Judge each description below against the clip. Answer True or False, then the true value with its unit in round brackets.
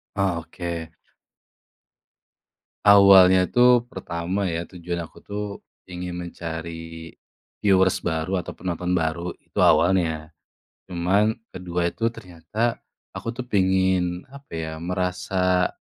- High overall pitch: False (90 Hz)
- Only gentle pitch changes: True (2.3 semitones)